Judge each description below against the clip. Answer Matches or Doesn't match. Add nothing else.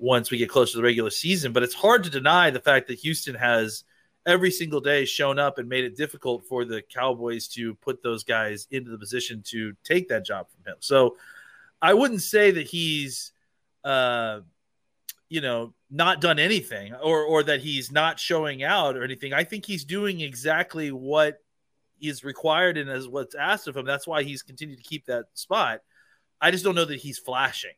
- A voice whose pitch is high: Doesn't match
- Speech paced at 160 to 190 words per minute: Doesn't match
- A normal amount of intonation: Matches